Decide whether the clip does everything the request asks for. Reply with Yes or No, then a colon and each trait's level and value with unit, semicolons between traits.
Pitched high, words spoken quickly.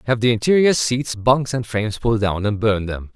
No: low, 115 Hz; fast, 230 wpm